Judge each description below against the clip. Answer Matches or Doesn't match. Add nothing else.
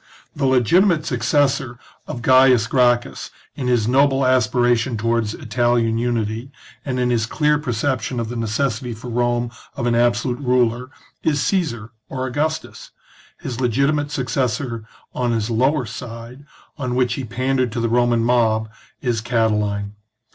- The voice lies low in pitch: Matches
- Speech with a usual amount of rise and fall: Doesn't match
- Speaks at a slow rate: Doesn't match